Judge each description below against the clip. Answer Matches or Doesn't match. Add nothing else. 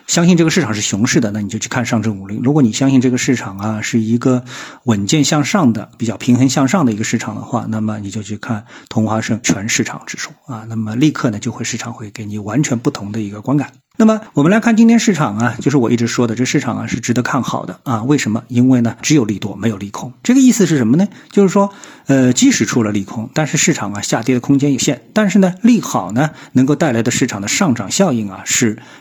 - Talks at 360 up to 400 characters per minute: Matches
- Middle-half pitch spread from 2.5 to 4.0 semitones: Doesn't match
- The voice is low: Matches